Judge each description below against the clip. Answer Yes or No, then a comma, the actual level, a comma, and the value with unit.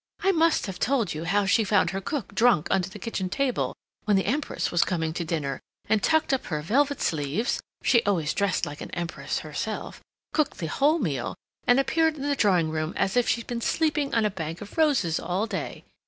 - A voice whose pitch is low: No, high, 205 Hz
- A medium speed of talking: No, fast, 215 wpm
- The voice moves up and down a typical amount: No, wide, 8.1 semitones